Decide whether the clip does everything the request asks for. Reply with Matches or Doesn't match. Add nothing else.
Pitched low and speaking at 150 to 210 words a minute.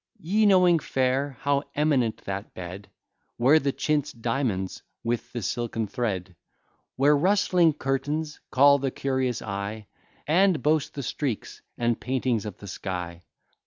Doesn't match